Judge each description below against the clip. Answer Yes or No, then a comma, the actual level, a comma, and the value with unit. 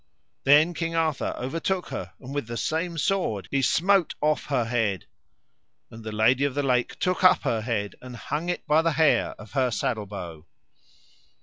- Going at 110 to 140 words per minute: No, average, 190 wpm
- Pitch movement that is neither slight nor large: No, wide, 6.3 semitones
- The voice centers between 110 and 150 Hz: Yes, low, 135 Hz